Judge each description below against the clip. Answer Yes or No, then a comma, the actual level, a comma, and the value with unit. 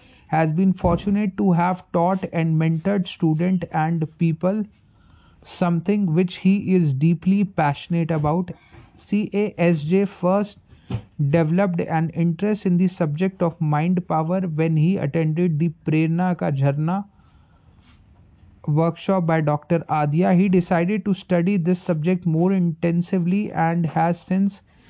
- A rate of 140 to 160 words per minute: No, average, 130 wpm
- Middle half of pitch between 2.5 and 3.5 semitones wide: Yes, average, 2.8 semitones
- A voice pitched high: No, medium, 170 Hz